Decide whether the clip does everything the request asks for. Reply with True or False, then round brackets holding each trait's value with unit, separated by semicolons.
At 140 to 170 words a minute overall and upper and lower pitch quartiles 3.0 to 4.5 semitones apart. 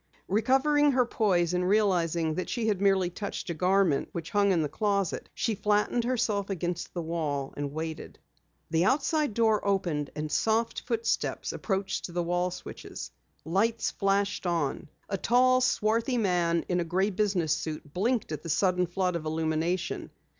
True (160 wpm; 4.2 semitones)